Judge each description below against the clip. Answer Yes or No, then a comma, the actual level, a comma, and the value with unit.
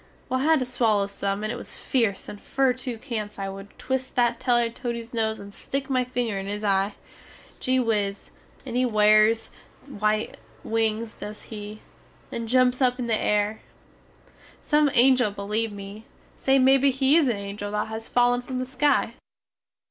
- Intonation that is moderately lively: Yes, average, 3.4 semitones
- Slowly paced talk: No, average, 180 wpm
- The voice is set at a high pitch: Yes, high, 230 Hz